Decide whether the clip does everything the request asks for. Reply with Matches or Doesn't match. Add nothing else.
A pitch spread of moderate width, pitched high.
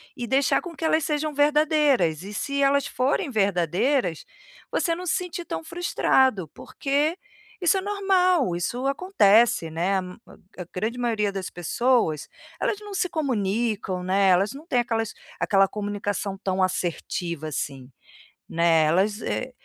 Doesn't match